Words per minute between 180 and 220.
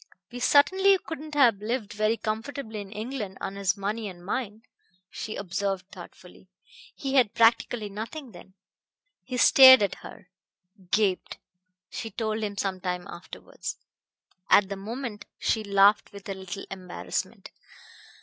No: average, 140 wpm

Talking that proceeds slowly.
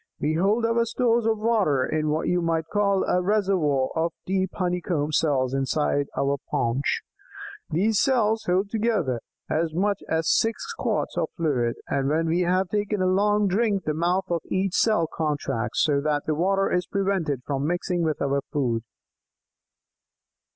No: average, 165 wpm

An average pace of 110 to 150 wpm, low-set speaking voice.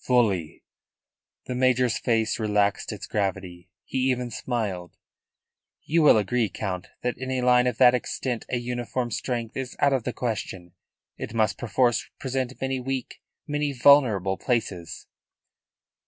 Yes: average, 140 wpm; low, 120 Hz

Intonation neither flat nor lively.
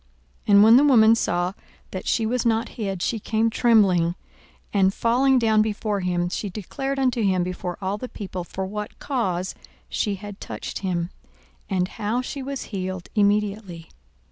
Yes: average, 3.6 semitones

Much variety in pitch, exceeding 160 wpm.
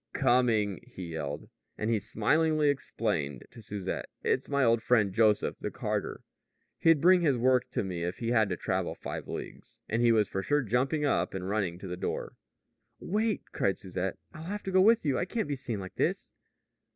Yes: wide, 6.9 semitones; average, 200 wpm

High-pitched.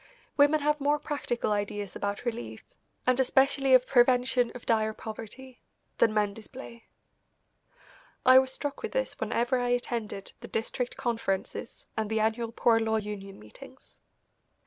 Yes: high, 235 Hz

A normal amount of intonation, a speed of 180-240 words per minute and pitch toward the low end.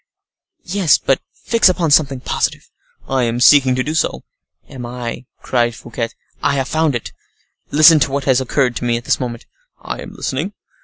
Yes: average, 3.8 semitones; average, 185 wpm; low, 130 Hz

